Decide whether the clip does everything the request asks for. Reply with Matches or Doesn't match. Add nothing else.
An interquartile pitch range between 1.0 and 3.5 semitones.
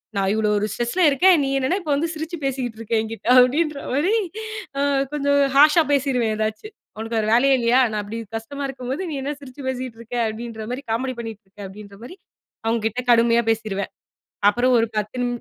Doesn't match